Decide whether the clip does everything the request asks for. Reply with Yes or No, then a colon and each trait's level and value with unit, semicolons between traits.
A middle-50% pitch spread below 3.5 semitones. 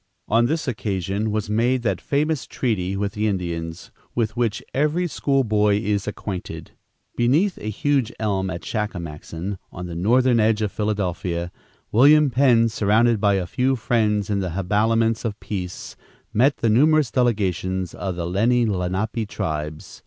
No: average, 4.2 semitones